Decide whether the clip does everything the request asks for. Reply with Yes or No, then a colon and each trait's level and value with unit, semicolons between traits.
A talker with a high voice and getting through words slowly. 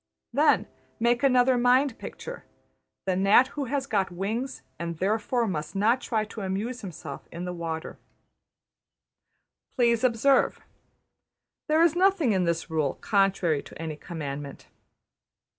Yes: high, 210 Hz; slow, 130 wpm